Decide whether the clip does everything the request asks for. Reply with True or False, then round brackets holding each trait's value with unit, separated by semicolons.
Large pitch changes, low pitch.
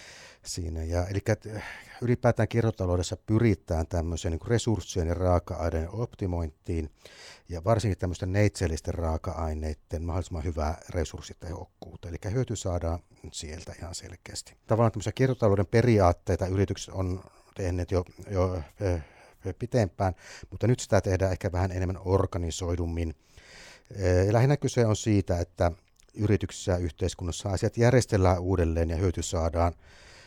False (3.2 semitones; 90 Hz)